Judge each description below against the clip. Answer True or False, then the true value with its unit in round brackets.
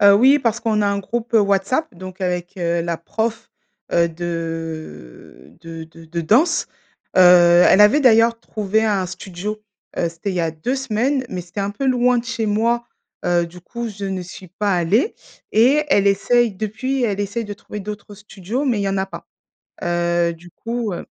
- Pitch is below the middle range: False (200 Hz)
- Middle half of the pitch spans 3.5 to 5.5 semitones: True (4.8 semitones)